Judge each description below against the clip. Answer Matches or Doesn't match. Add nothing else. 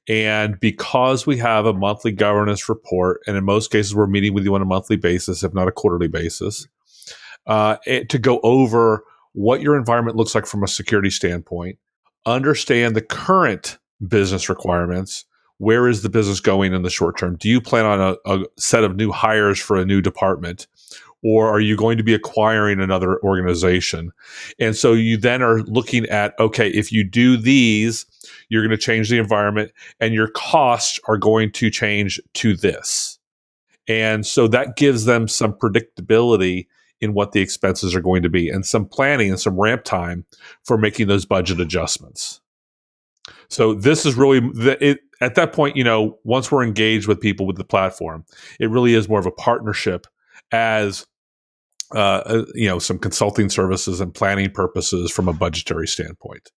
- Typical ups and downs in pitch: Matches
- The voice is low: Matches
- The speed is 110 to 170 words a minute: Doesn't match